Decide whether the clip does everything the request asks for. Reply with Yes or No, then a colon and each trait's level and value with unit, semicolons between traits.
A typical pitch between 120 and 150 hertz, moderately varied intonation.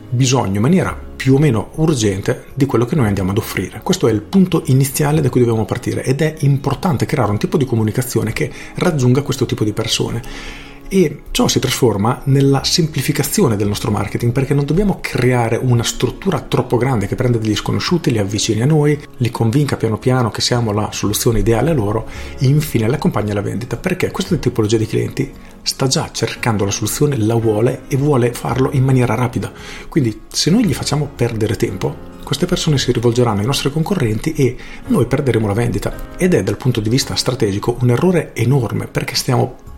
Yes: low, 125 Hz; average, 4.5 semitones